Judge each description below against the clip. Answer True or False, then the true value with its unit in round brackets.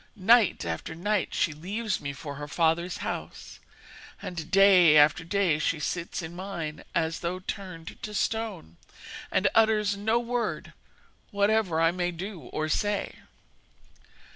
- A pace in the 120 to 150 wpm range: True (140 wpm)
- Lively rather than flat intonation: False (4.2 semitones)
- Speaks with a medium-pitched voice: True (180 Hz)